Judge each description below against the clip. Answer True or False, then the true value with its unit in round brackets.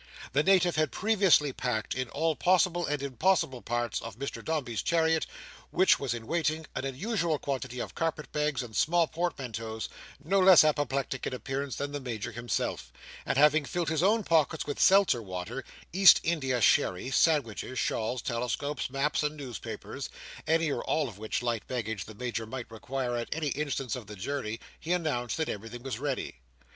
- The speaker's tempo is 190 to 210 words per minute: False (175 wpm)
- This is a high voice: False (140 Hz)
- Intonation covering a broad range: False (5.0 semitones)